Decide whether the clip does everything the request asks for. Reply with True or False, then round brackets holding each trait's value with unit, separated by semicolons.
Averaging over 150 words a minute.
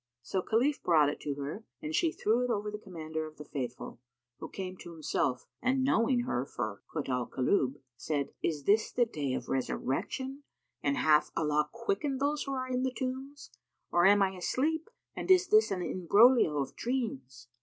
True (185 wpm)